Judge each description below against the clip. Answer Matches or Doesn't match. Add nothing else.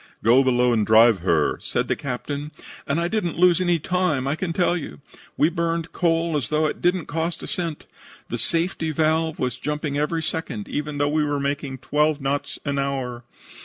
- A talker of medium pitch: Matches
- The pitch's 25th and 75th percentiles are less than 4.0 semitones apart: Matches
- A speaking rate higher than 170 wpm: Matches